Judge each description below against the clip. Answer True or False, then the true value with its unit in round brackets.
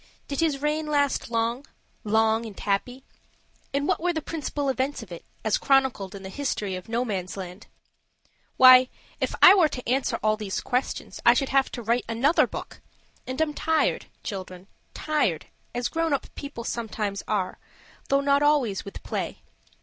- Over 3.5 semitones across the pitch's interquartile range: True (5.2 semitones)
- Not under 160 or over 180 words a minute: True (165 wpm)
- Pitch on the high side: True (250 Hz)